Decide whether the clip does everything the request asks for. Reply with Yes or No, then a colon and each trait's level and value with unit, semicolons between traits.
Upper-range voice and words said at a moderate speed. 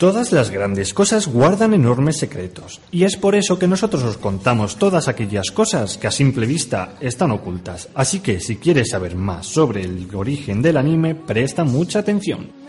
No: low, 135 Hz; average, 180 wpm